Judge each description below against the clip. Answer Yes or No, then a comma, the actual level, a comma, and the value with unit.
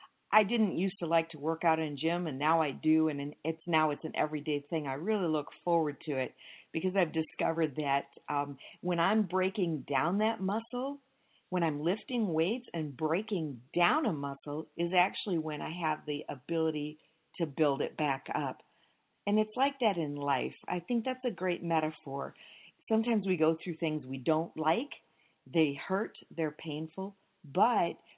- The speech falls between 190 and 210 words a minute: No, average, 180 wpm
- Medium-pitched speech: Yes, medium, 165 Hz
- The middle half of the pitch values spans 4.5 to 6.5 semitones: No, average, 3.5 semitones